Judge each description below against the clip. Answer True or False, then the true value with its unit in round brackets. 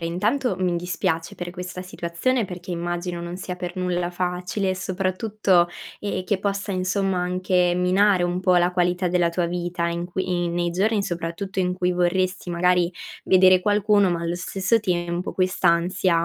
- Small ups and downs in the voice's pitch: True (1.3 semitones)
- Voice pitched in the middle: True (180 Hz)